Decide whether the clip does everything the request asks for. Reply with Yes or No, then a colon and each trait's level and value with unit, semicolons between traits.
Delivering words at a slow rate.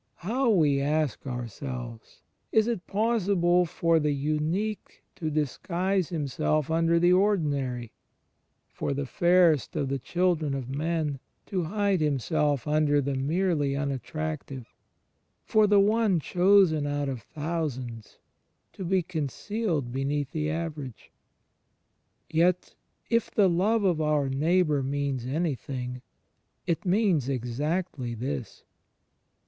Yes: slow, 120 wpm